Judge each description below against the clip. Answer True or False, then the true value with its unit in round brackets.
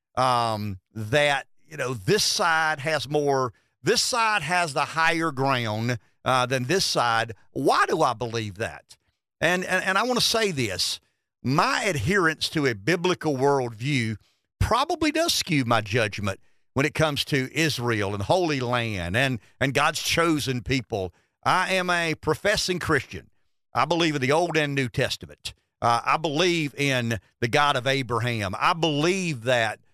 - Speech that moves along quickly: False (160 wpm)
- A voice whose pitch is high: False (135 Hz)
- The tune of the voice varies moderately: False (5.7 semitones)